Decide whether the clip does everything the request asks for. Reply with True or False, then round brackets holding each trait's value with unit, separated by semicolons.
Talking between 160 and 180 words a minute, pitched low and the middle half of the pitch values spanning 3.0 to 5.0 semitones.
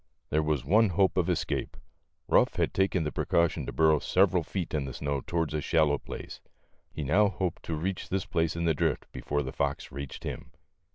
False (205 wpm; 80 Hz; 3.6 semitones)